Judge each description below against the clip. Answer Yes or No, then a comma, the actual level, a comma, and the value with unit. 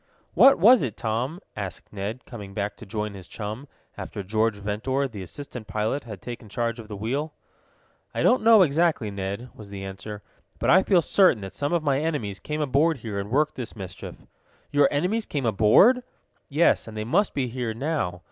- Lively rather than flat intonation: Yes, wide, 6.2 semitones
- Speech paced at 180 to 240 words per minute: Yes, average, 195 wpm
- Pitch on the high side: No, low, 115 Hz